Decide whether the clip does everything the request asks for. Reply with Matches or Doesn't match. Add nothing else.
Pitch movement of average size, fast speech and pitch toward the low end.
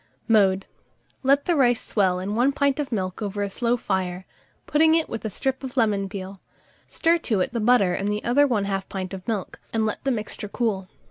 Doesn't match